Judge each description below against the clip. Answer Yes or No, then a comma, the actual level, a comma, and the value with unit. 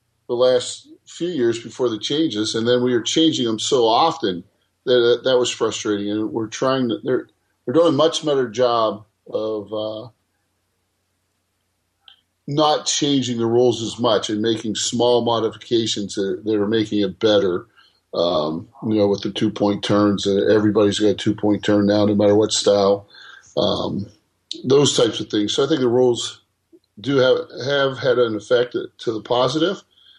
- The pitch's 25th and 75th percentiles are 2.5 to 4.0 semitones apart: Yes, average, 3.5 semitones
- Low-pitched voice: Yes, low, 110 Hz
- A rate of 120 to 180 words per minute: Yes, average, 175 wpm